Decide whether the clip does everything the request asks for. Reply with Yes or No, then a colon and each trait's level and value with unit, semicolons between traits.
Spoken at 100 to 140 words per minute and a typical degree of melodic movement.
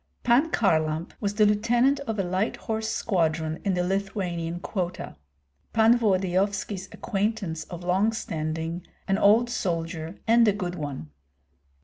Yes: slow, 135 wpm; average, 4.5 semitones